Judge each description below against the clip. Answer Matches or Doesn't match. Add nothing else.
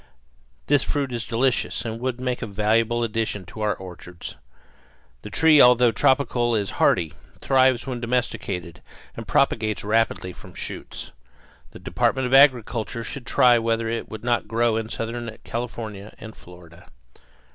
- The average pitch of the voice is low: Matches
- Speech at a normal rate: Matches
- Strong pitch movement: Doesn't match